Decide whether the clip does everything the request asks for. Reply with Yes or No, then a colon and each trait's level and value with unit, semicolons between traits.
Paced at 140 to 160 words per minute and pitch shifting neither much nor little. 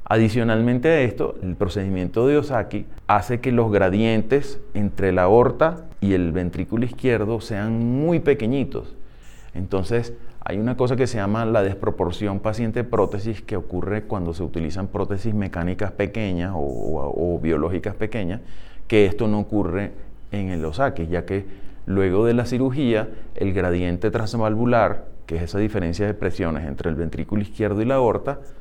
Yes: average, 150 wpm; average, 3.8 semitones